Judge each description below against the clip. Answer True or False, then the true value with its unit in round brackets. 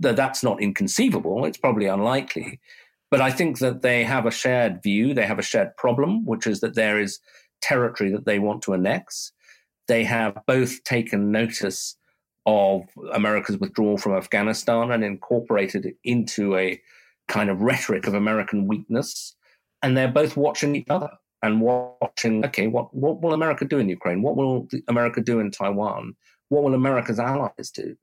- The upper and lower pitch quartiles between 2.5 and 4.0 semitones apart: False (4.5 semitones)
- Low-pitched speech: True (120 Hz)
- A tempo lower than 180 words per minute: True (170 wpm)